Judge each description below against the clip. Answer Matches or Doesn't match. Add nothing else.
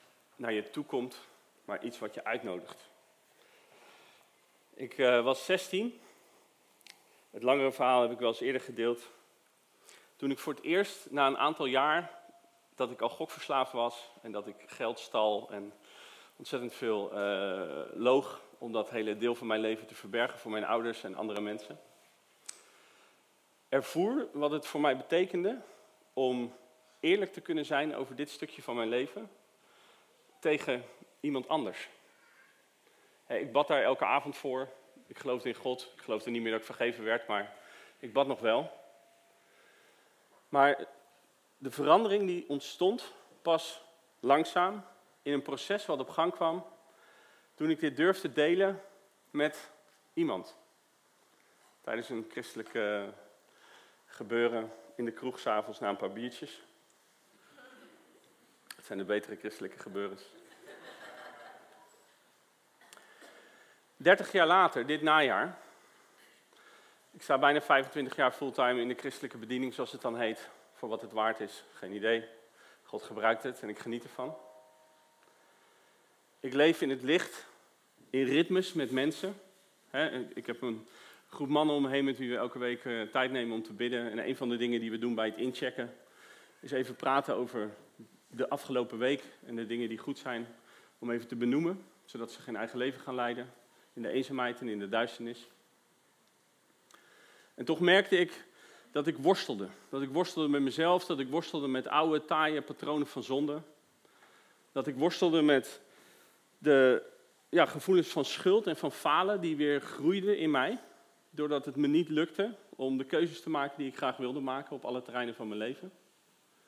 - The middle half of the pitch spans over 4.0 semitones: Matches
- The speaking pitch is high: Doesn't match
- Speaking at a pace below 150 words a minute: Doesn't match